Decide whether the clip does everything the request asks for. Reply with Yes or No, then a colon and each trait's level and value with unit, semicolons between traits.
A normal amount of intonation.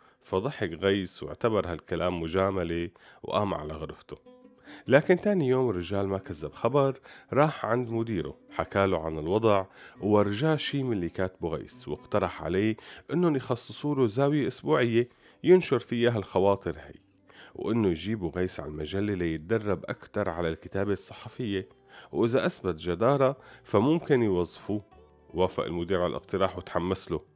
No: wide, 6.2 semitones